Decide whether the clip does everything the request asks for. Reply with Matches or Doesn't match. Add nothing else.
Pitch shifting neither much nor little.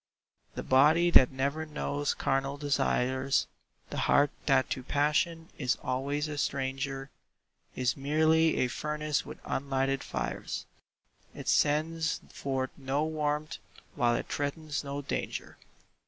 Doesn't match